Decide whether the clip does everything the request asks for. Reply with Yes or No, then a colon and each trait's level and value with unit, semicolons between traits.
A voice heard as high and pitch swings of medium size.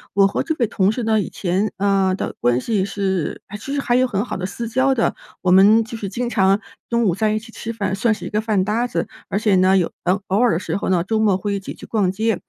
Yes: high, 205 Hz; average, 3.0 semitones